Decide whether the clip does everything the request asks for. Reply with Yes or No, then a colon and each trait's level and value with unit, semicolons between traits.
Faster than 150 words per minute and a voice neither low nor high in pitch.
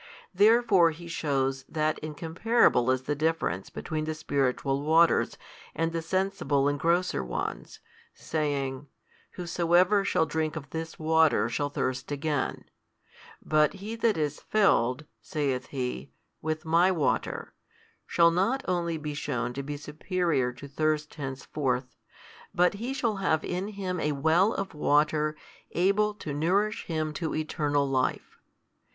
No: slow, 135 wpm; medium, 155 Hz